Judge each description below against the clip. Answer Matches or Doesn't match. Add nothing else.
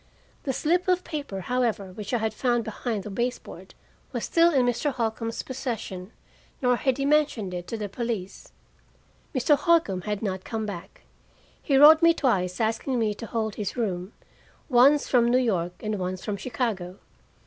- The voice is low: Doesn't match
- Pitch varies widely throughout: Doesn't match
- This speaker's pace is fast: Doesn't match